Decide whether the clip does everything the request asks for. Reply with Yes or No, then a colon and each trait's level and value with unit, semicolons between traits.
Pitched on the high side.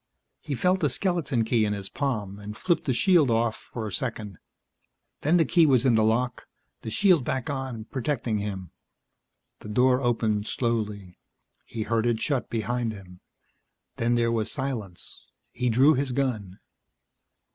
No: low, 120 Hz